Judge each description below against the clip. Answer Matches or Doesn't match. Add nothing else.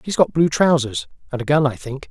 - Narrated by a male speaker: Matches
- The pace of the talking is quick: Matches